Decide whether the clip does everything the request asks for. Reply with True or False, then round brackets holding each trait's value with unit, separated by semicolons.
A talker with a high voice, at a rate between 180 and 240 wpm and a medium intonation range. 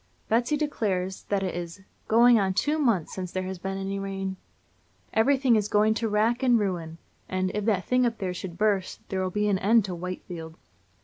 True (195 Hz; 195 wpm; 3.3 semitones)